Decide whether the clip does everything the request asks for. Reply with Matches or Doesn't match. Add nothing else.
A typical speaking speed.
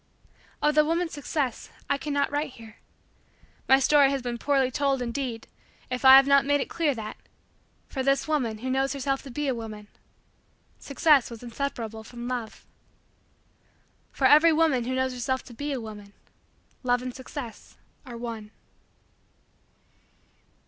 Matches